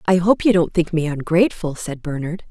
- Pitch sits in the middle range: Yes, medium, 170 Hz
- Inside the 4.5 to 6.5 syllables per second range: Yes, 5.5 syllables/s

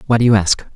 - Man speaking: Yes, male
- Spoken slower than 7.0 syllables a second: No, 7.4 syllables/s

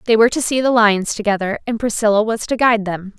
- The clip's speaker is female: Yes, female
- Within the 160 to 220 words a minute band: No, fast, 245 wpm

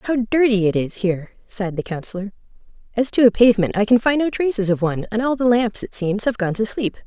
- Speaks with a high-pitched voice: Yes, high, 215 Hz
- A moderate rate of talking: No, fast, 245 wpm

